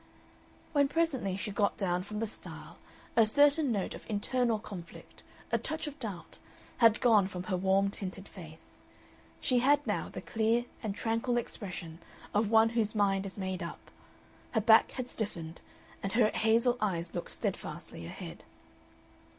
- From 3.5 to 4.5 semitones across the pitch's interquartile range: Yes, average, 3.9 semitones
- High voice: Yes, high, 215 Hz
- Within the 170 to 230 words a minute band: No, average, 160 wpm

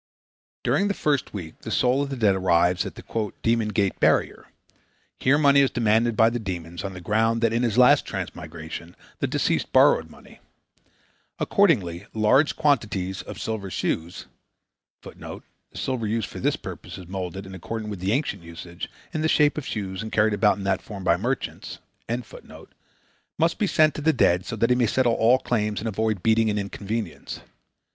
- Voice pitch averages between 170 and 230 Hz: No, low, 110 Hz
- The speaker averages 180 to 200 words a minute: Yes, average, 185 wpm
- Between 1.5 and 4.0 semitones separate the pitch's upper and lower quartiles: No, average, 4.5 semitones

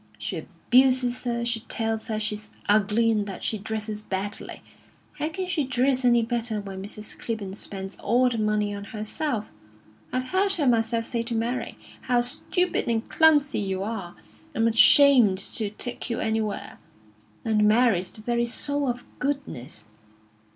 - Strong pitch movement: No, average, 3.0 semitones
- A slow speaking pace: No, average, 160 wpm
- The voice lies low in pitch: No, high, 225 Hz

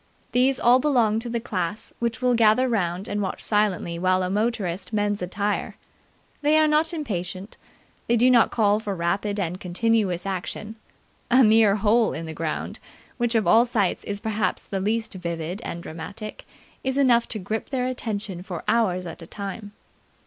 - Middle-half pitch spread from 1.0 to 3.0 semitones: No, average, 4.1 semitones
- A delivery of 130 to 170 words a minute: No, average, 180 wpm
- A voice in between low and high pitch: No, high, 210 Hz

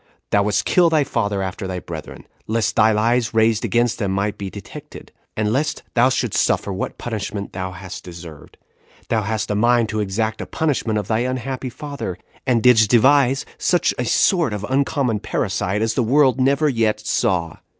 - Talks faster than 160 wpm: Yes, average, 180 wpm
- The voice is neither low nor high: No, low, 110 Hz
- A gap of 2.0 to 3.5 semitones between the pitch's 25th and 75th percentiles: No, average, 4.0 semitones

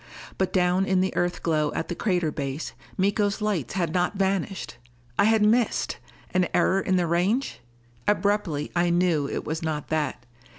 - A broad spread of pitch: No, average, 3.5 semitones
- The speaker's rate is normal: Yes, average, 170 wpm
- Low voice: No, medium, 180 Hz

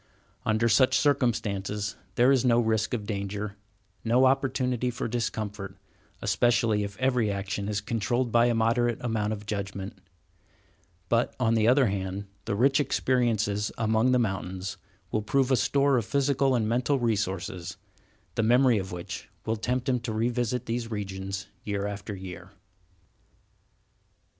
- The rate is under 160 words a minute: Yes, average, 145 wpm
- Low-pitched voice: Yes, low, 110 Hz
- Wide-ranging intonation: No, average, 3.4 semitones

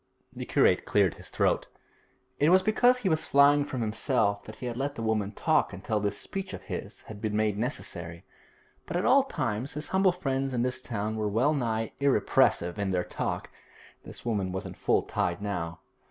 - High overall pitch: No, low, 115 Hz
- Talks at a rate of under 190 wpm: No, average, 200 wpm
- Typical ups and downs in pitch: No, wide, 6.0 semitones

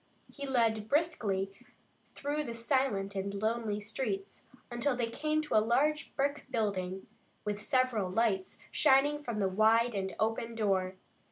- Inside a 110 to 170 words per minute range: Yes, average, 145 wpm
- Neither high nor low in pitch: No, high, 225 Hz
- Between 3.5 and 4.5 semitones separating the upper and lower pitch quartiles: No, average, 4.9 semitones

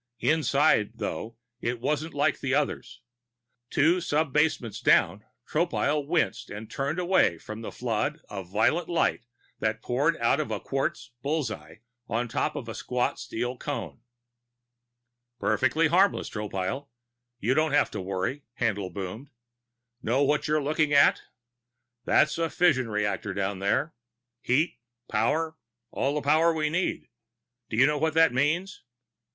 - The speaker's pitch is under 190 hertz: Yes, medium, 140 Hz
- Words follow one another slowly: No, average, 145 wpm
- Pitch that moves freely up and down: Yes, wide, 5.8 semitones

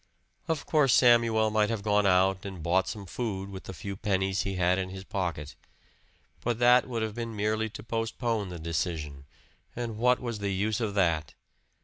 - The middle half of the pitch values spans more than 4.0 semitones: No, average, 3.4 semitones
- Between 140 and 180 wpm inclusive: No, average, 190 wpm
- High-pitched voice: No, low, 100 Hz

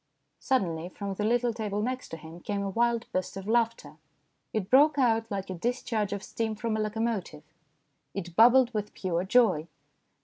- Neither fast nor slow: Yes, average, 175 wpm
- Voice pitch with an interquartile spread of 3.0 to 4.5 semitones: Yes, average, 3.9 semitones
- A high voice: Yes, high, 215 Hz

